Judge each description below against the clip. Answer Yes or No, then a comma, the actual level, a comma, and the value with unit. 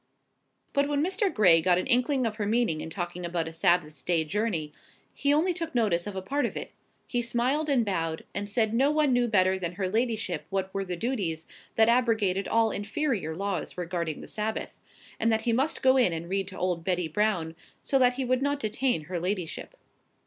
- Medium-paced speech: No, fast, 210 wpm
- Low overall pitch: No, high, 210 Hz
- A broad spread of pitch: Yes, wide, 5.8 semitones